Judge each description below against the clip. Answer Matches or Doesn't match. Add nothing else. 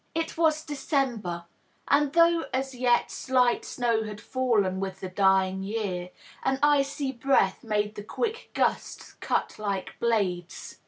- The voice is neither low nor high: Doesn't match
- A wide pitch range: Matches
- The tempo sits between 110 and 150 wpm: Matches